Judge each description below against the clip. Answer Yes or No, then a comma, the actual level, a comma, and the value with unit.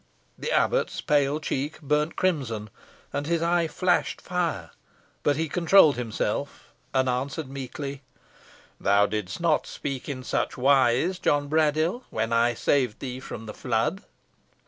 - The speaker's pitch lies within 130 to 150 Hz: Yes, medium, 140 Hz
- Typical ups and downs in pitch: Yes, average, 4.5 semitones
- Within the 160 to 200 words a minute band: No, average, 140 wpm